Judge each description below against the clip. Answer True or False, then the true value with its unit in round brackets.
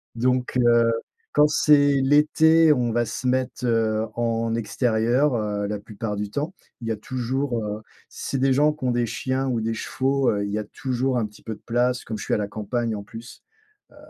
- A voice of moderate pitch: False (120 Hz)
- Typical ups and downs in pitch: True (3.1 semitones)